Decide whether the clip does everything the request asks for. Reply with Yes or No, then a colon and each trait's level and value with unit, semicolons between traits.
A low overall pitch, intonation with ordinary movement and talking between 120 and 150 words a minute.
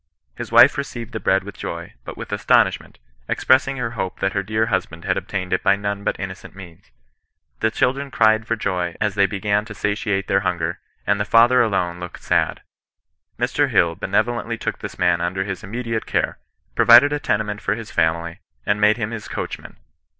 No: low, 100 Hz; average, 3.4 semitones; average, 190 wpm